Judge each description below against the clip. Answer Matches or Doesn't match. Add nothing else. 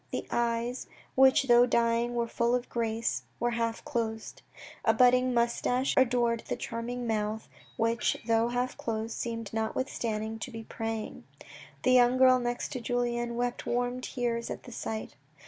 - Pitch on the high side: Matches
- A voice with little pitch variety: Matches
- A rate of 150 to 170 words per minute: Matches